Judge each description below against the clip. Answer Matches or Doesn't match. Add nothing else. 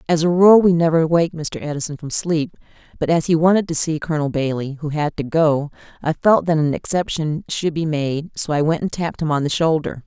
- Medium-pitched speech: Matches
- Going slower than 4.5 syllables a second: Doesn't match